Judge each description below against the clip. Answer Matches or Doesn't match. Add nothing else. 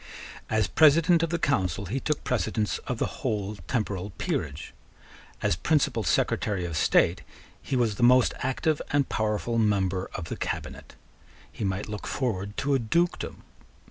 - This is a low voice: Matches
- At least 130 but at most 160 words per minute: Matches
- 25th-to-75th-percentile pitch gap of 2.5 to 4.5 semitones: Doesn't match